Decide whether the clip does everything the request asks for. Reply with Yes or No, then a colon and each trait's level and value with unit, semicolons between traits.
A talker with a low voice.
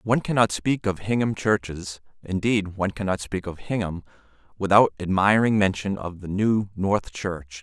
Yes: low, 100 Hz